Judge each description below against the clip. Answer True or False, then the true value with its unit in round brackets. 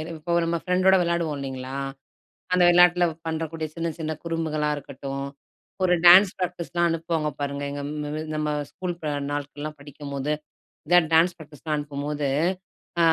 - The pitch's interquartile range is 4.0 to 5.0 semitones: False (2.9 semitones)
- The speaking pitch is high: False (155 Hz)